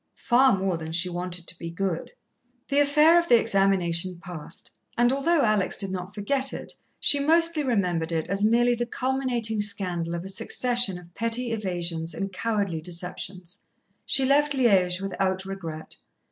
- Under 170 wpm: Yes, average, 160 wpm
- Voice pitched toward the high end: Yes, high, 195 Hz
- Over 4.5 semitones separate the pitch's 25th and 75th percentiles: Yes, wide, 5.4 semitones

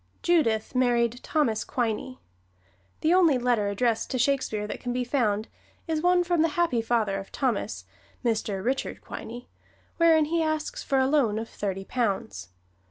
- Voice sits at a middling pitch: No, high, 245 Hz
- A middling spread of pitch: No, wide, 5.7 semitones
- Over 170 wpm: No, average, 160 wpm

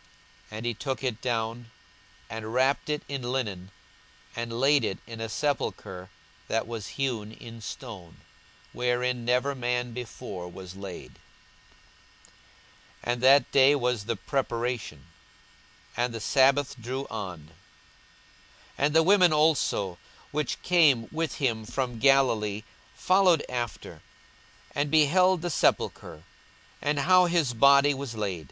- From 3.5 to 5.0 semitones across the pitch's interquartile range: Yes, average, 4.0 semitones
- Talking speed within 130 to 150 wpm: Yes, slow, 135 wpm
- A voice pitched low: Yes, low, 125 Hz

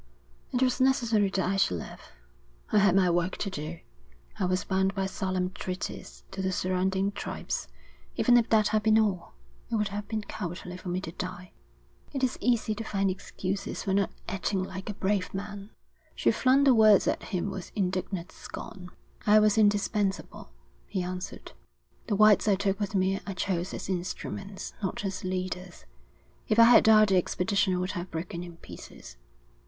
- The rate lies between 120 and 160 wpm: No, average, 180 wpm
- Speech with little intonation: Yes, narrow, 2.3 semitones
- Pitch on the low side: No, high, 195 Hz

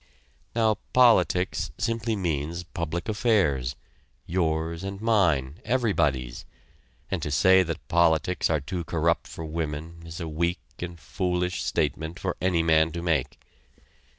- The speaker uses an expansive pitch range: No, average, 2.9 semitones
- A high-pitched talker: No, very low, 85 Hz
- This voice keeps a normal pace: No, slow, 130 wpm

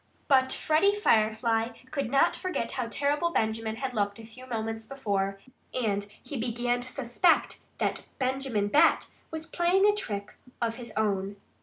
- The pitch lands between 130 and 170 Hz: No, high, 240 Hz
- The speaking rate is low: No, average, 155 wpm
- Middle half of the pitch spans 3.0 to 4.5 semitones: Yes, average, 4.1 semitones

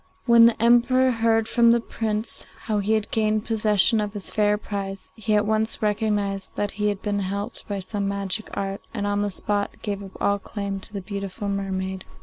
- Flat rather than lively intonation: Yes, narrow, 1.8 semitones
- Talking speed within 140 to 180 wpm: No, average, 200 wpm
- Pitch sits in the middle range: No, high, 205 Hz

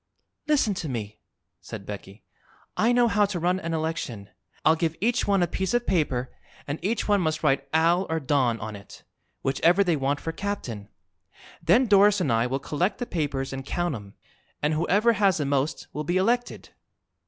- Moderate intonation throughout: No, wide, 6.5 semitones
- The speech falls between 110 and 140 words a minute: No, average, 190 wpm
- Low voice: No, medium, 160 Hz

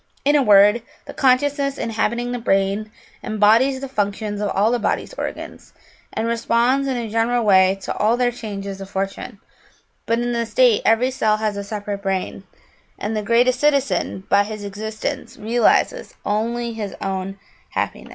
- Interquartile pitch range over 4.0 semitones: No, average, 3.1 semitones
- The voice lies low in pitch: No, high, 220 Hz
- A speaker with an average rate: Yes, average, 165 wpm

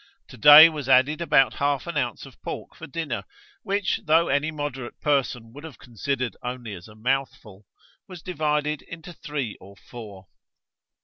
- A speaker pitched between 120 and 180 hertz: Yes, medium, 140 Hz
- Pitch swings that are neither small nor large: Yes, average, 4.3 semitones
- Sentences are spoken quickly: No, average, 165 wpm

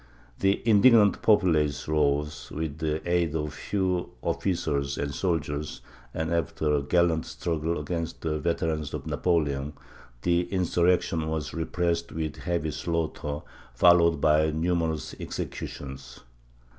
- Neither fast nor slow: No, slow, 120 wpm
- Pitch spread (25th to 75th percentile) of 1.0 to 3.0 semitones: Yes, narrow, 2.5 semitones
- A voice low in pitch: Yes, very low, 80 Hz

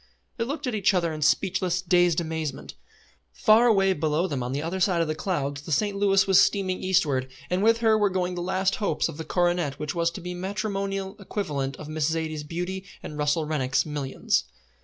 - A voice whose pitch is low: No, medium, 175 Hz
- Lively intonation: No, average, 4.0 semitones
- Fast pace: Yes, fast, 210 wpm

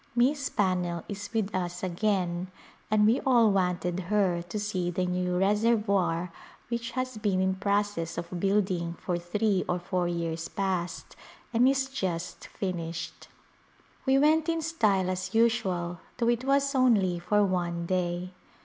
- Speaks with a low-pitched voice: No, high, 190 Hz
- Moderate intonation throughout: Yes, average, 4.1 semitones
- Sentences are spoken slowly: No, average, 150 wpm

